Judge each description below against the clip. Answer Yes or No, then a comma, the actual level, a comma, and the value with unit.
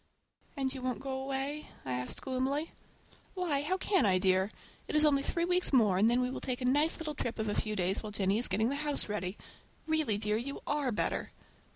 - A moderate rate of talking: No, fast, 225 wpm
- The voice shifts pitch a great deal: Yes, wide, 5.7 semitones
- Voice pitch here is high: Yes, very high, 255 Hz